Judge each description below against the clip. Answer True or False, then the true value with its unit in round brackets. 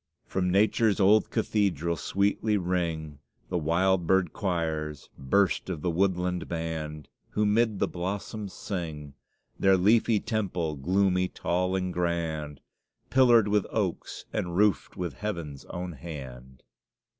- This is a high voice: False (90 Hz)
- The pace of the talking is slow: True (125 wpm)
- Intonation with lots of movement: False (3.6 semitones)